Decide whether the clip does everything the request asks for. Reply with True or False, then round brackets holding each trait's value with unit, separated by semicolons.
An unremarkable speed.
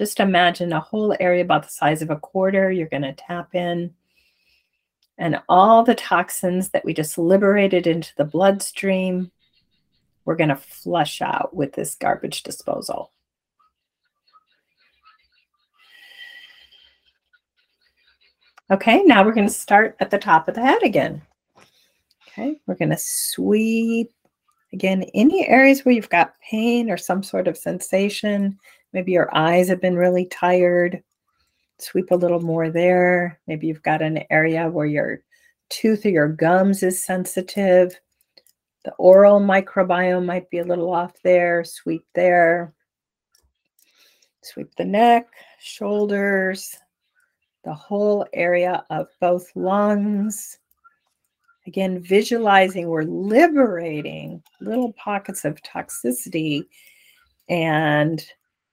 False (120 wpm)